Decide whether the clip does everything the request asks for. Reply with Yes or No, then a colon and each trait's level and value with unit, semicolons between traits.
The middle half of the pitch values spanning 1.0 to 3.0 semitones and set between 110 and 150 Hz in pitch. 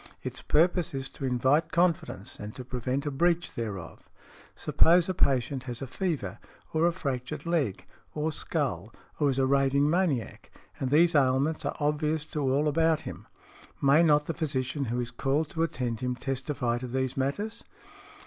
No: average, 3.8 semitones; medium, 140 Hz